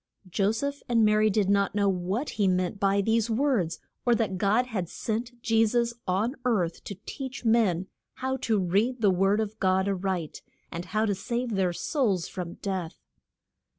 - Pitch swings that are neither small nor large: Yes, average, 3.6 semitones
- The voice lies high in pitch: Yes, high, 205 Hz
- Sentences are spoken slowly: No, average, 185 wpm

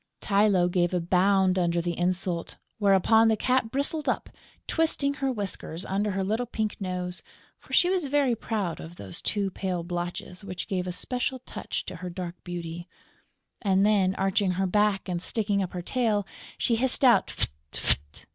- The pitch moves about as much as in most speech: Yes, average, 3.7 semitones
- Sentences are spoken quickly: No, average, 175 wpm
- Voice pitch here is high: Yes, high, 195 Hz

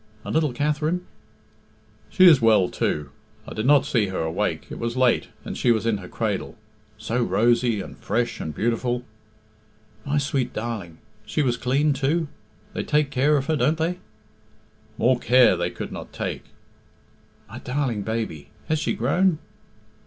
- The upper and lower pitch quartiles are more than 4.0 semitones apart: Yes, average, 4.6 semitones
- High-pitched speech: No, low, 125 Hz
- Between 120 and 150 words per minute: No, average, 160 wpm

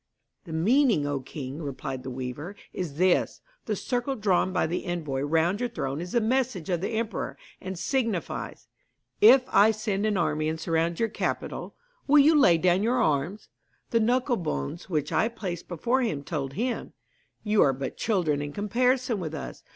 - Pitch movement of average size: No, wide, 6.9 semitones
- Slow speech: No, average, 180 wpm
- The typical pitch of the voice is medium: Yes, medium, 180 Hz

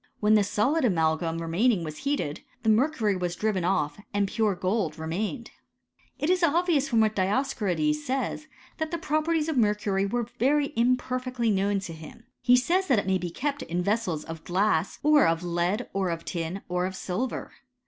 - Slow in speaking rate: No, average, 180 wpm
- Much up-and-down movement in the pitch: Yes, wide, 6.7 semitones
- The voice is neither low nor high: No, high, 210 Hz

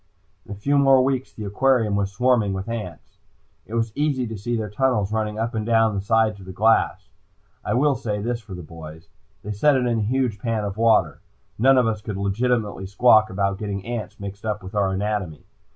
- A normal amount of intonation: Yes, average, 3.2 semitones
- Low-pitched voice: Yes, low, 110 Hz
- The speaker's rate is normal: No, fast, 215 wpm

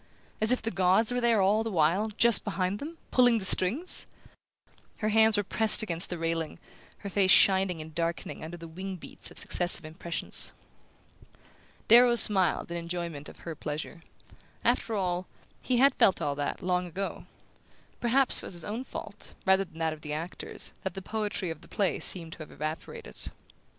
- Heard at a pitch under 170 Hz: No, medium, 185 Hz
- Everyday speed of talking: Yes, average, 180 wpm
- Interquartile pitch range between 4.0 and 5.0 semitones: Yes, average, 4.5 semitones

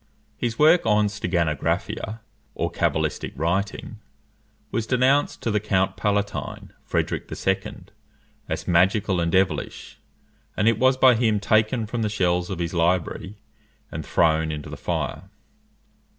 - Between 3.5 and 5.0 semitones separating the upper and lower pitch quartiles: Yes, average, 4.3 semitones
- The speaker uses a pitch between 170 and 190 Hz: No, low, 105 Hz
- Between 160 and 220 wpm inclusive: No, slow, 135 wpm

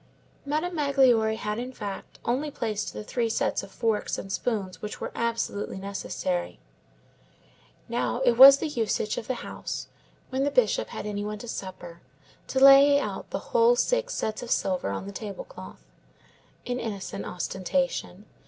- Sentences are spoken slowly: No, average, 160 wpm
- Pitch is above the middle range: Yes, high, 230 Hz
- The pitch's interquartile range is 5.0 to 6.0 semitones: Yes, average, 5.3 semitones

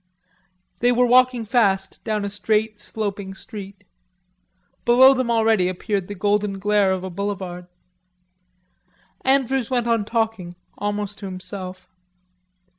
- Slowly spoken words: Yes, slow, 120 wpm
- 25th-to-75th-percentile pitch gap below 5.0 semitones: Yes, average, 3.2 semitones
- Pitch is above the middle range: Yes, high, 205 Hz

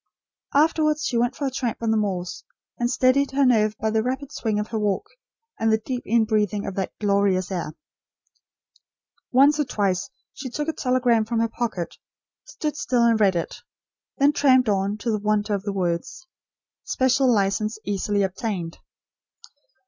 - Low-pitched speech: No, high, 220 Hz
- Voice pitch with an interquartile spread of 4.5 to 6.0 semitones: No, average, 4.1 semitones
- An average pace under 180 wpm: Yes, average, 170 wpm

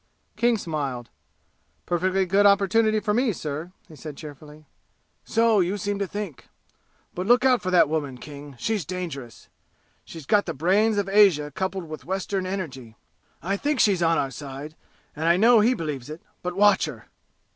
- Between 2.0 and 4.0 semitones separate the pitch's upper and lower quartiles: No, average, 5.2 semitones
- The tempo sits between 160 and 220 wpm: Yes, average, 170 wpm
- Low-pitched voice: No, medium, 180 Hz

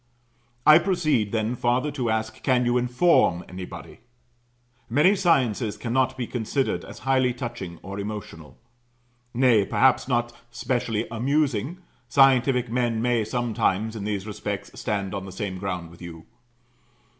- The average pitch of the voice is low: Yes, low, 120 Hz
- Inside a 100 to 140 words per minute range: Yes, slow, 135 wpm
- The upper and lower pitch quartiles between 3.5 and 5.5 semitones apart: Yes, average, 4.1 semitones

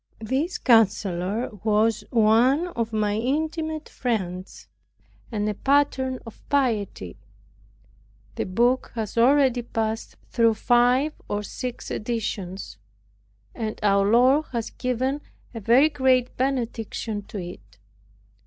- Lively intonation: No, average, 3.6 semitones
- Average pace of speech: No, slow, 110 wpm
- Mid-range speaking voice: No, high, 230 Hz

